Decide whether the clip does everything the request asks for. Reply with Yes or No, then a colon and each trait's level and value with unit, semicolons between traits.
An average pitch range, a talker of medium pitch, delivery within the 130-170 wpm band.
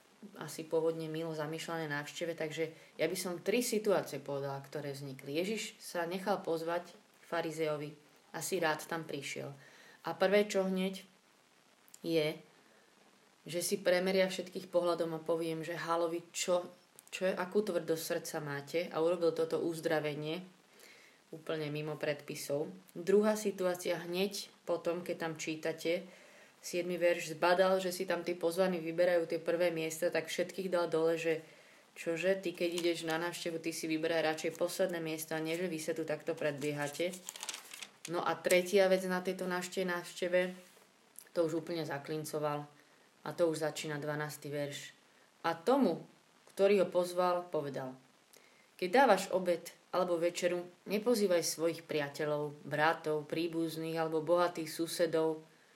No: narrow, 2.1 semitones; medium, 170 Hz; average, 140 wpm